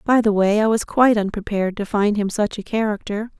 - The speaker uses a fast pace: Yes, fast, 230 wpm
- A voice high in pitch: Yes, high, 210 Hz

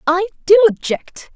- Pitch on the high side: Yes, very high, 325 Hz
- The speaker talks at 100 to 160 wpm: Yes, slow, 135 wpm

